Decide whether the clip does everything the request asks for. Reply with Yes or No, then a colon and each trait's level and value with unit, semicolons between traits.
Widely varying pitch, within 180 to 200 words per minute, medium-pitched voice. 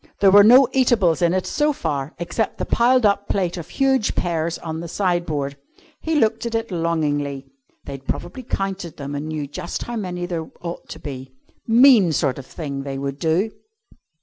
Yes: wide, 6.9 semitones; average, 185 wpm; medium, 175 Hz